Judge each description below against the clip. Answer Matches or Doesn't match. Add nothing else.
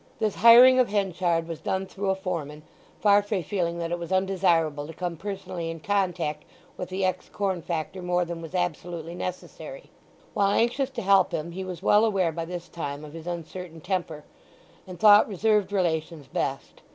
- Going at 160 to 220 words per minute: Matches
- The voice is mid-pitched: Matches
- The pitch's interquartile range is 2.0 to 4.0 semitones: Matches